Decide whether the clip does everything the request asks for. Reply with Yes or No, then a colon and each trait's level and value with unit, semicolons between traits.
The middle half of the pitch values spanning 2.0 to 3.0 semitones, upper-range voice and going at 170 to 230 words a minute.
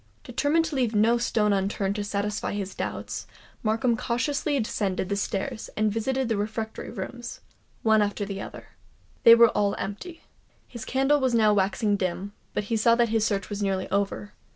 Yes: average, 2.7 semitones; high, 215 Hz; average, 175 wpm